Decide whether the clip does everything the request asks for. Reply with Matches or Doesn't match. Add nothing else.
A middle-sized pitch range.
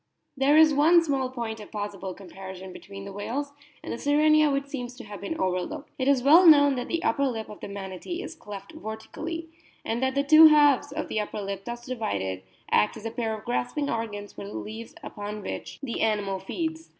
Doesn't match